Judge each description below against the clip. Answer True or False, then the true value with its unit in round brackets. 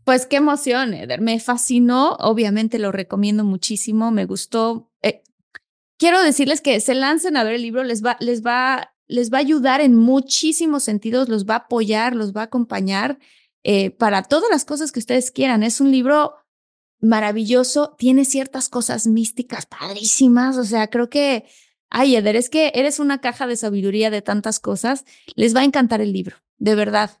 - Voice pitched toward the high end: True (245 Hz)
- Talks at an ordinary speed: True (180 wpm)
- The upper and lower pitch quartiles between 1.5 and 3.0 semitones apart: False (3.5 semitones)